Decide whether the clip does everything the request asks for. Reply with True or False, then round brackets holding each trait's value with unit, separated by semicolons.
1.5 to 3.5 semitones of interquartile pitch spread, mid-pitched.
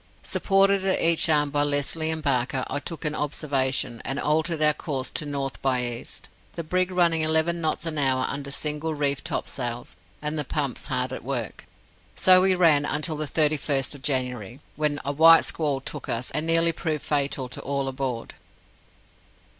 True (2.8 semitones; 150 Hz)